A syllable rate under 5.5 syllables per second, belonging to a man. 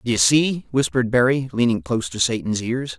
Yes: 5.3 syllables/s; male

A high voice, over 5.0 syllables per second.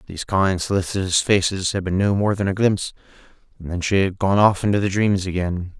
No: very low, 95 Hz; 5.9 syllables/s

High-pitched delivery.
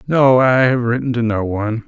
No: low, 120 Hz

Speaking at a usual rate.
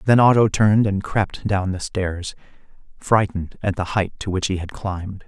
Yes: average, 195 wpm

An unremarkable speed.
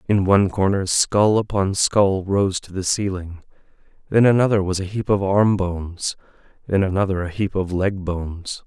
Yes: average, 175 wpm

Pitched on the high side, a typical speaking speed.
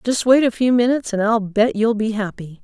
No: high, 225 Hz; fast, 250 wpm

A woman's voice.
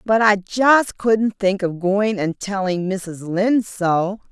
Yes: female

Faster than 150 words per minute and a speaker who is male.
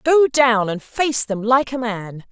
No: fast, 205 wpm; female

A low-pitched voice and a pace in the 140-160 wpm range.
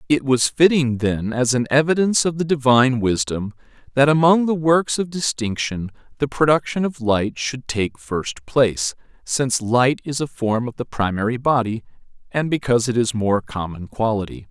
No: low, 125 Hz; average, 170 wpm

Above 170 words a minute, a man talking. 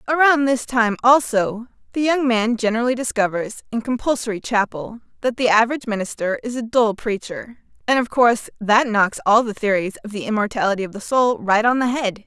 No: average, 185 wpm; female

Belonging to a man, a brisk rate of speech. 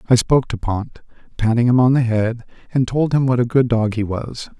Yes: male; fast, 235 wpm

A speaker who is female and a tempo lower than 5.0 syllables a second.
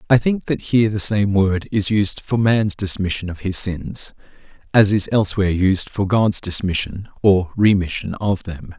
No: male; 4.6 syllables/s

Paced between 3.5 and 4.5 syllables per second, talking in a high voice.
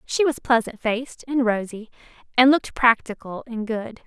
No: 5.0 syllables/s; high, 235 Hz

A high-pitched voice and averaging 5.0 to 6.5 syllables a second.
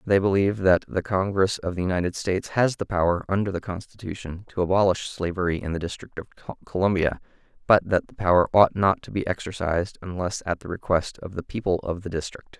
No: very low, 90 Hz; 6.0 syllables/s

